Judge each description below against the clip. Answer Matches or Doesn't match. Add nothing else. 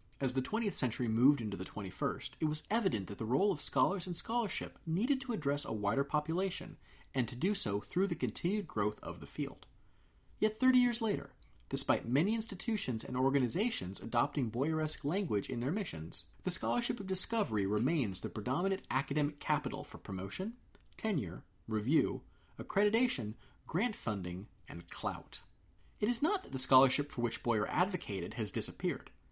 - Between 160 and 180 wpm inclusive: Matches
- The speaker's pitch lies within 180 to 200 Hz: Doesn't match